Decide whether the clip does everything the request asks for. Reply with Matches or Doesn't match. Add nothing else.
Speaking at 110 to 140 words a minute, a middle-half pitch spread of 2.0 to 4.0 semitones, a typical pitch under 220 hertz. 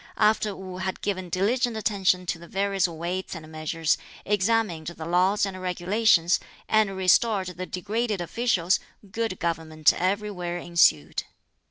Matches